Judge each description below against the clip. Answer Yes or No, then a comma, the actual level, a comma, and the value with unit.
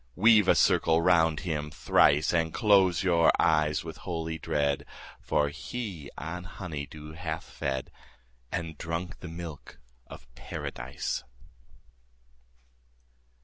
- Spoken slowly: Yes, slow, 120 wpm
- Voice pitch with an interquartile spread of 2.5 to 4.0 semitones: Yes, average, 2.8 semitones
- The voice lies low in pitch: Yes, very low, 80 Hz